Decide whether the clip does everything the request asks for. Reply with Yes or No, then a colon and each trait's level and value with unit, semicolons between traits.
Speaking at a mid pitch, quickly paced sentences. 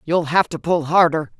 Yes: medium, 160 Hz; fast, 215 wpm